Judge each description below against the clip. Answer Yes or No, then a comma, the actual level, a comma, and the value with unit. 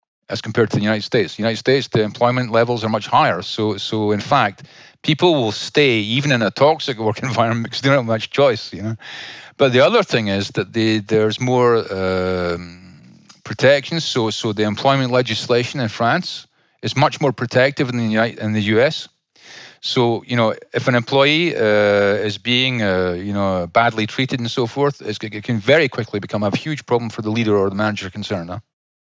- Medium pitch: No, low, 115 Hz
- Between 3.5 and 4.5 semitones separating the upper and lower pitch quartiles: No, average, 3.1 semitones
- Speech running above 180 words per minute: Yes, average, 200 wpm